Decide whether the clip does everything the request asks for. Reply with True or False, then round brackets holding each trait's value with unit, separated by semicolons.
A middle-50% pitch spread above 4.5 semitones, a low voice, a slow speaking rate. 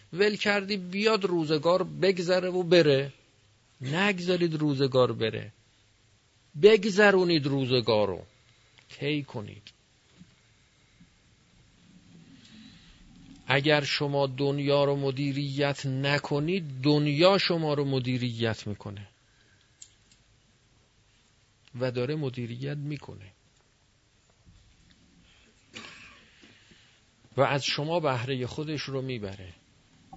True (5.0 semitones; 130 Hz; 75 wpm)